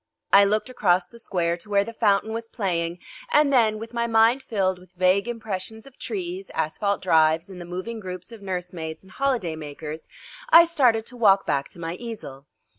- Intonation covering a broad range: No, average, 4.6 semitones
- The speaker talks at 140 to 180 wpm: No, average, 190 wpm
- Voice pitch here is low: No, high, 200 Hz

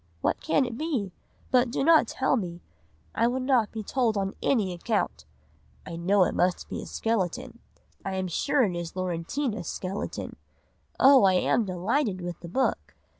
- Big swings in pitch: Yes, wide, 5.9 semitones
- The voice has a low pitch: No, high, 205 Hz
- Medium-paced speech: Yes, average, 175 wpm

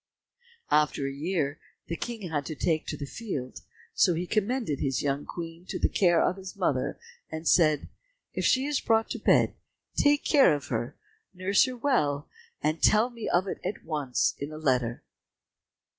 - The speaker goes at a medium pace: Yes, average, 175 wpm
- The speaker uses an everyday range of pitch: No, wide, 6.7 semitones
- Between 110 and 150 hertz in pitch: No, medium, 165 Hz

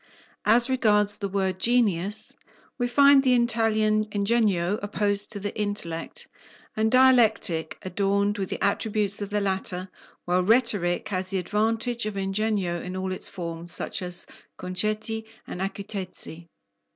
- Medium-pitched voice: No, high, 205 Hz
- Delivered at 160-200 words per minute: No, average, 140 wpm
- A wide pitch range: No, average, 2.9 semitones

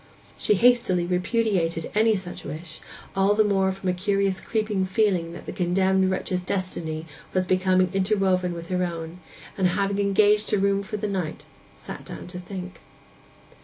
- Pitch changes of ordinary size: No, narrow, 1.8 semitones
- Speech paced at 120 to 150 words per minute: No, average, 165 wpm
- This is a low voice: No, high, 190 Hz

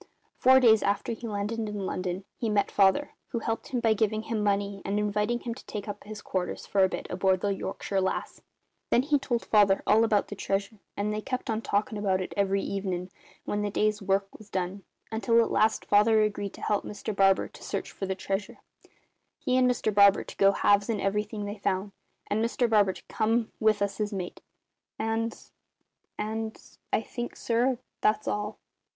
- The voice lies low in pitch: No, high, 210 Hz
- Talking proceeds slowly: No, average, 200 wpm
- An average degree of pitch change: No, narrow, 2.0 semitones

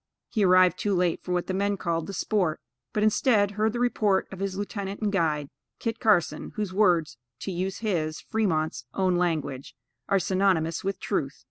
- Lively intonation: No, average, 3.2 semitones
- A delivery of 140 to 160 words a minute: No, average, 185 wpm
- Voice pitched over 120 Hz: Yes, high, 190 Hz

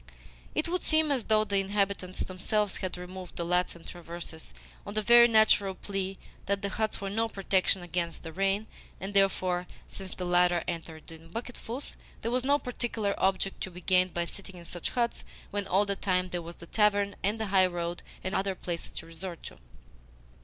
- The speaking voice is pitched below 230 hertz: Yes, high, 190 Hz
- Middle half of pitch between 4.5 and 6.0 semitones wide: No, average, 2.9 semitones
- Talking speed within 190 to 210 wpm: Yes, average, 195 wpm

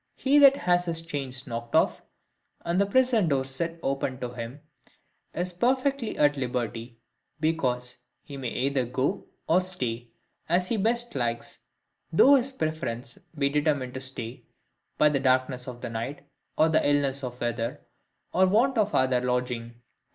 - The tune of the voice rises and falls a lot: Yes, wide, 6.1 semitones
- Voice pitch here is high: No, medium, 140 Hz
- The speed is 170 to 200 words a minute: No, average, 160 wpm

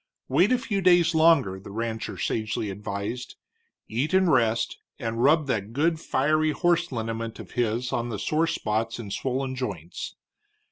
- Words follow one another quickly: No, average, 155 wpm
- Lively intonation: Yes, wide, 5.8 semitones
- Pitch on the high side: No, low, 125 Hz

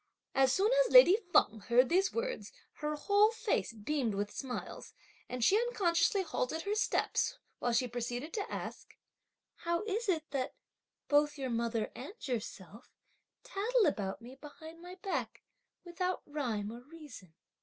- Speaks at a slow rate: No, average, 155 wpm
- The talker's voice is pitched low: No, very high, 300 Hz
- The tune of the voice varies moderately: No, wide, 8.1 semitones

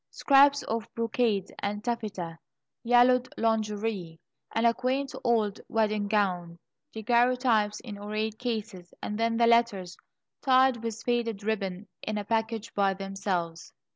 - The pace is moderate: No, slow, 130 wpm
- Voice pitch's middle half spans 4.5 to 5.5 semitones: No, average, 2.7 semitones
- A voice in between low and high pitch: No, high, 220 Hz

